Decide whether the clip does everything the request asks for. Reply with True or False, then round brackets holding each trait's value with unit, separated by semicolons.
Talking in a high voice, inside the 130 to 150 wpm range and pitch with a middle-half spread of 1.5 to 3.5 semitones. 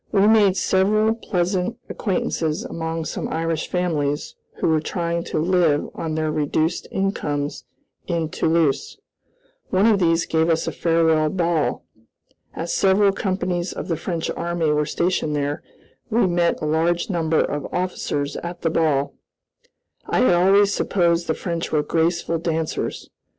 False (170 Hz; 145 wpm; 2.6 semitones)